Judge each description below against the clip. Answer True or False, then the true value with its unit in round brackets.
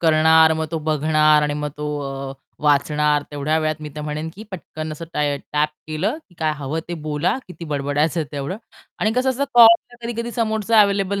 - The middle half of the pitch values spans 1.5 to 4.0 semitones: False (4.8 semitones)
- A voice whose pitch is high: False (155 Hz)